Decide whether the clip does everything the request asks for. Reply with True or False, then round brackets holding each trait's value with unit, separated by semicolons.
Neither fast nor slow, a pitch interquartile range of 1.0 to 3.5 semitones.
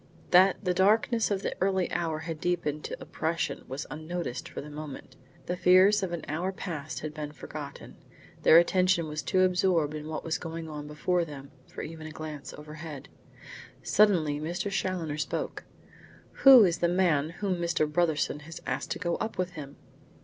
True (175 wpm; 3.2 semitones)